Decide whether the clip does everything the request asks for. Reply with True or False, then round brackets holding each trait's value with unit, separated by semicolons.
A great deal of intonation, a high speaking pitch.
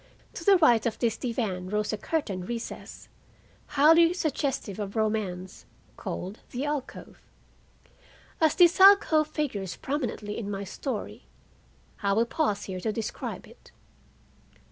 True (6.9 semitones; 230 Hz)